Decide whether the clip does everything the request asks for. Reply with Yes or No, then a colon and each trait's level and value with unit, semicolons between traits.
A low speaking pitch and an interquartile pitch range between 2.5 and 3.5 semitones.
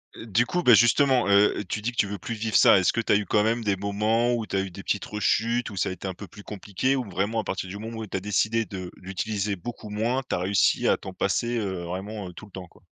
Yes: low, 105 Hz; average, 2.9 semitones